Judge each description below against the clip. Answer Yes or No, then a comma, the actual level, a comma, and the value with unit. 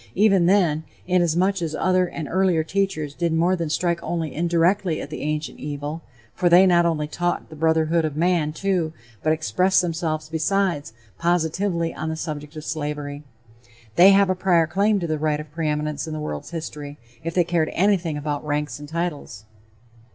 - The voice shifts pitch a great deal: No, average, 2.7 semitones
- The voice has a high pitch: No, medium, 165 Hz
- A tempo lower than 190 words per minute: Yes, average, 180 wpm